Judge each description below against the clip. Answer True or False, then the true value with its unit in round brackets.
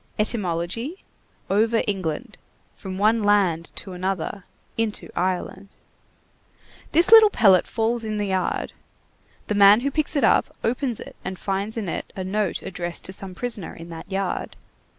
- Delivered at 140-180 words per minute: True (150 wpm)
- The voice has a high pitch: True (200 Hz)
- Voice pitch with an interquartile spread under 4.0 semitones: True (3.4 semitones)